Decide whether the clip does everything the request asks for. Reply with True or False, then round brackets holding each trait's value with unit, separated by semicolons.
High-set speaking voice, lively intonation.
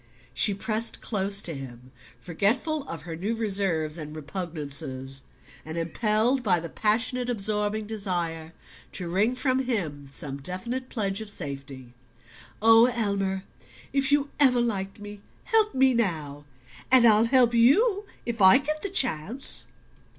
True (205 Hz; 6.8 semitones)